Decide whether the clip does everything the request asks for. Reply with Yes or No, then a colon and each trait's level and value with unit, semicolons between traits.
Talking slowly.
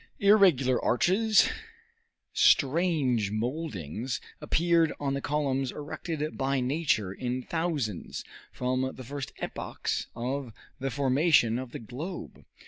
Yes: slow, 110 wpm